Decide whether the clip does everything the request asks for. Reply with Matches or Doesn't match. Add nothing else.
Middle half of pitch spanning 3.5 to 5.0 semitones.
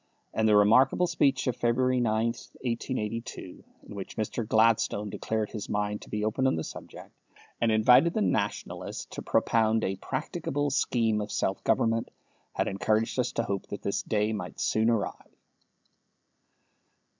Doesn't match